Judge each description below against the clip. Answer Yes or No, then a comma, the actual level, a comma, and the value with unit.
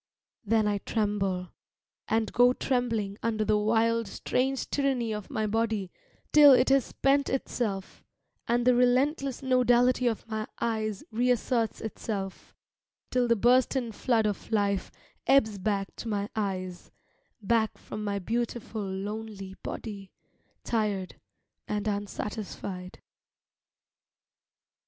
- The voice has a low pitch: No, high, 220 Hz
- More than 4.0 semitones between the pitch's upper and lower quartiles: No, average, 3.2 semitones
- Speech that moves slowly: Yes, slow, 115 wpm